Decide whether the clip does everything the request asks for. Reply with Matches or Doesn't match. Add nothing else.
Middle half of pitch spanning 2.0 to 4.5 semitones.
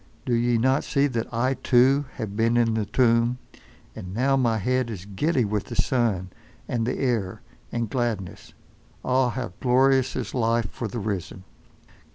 Matches